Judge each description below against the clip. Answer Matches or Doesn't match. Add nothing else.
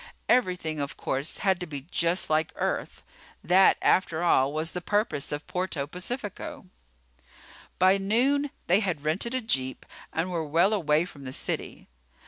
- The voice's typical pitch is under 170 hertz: Doesn't match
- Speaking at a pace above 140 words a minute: Matches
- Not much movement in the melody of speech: Doesn't match